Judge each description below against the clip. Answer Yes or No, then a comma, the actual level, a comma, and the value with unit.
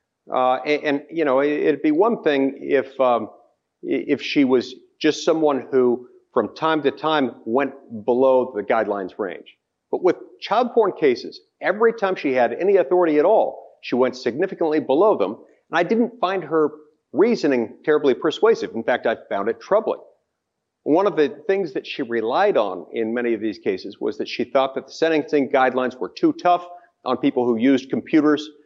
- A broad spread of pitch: Yes, wide, 8.5 semitones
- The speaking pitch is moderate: Yes, medium, 150 Hz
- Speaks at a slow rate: No, average, 180 wpm